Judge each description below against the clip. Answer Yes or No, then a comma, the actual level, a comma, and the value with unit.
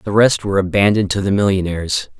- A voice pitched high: No, low, 100 Hz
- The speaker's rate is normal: Yes, average, 190 wpm